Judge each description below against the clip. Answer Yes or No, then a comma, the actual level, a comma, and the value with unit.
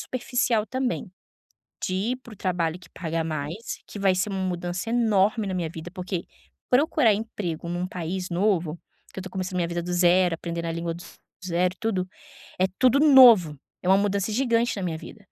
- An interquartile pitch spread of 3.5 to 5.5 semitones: Yes, average, 3.9 semitones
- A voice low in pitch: No, medium, 185 Hz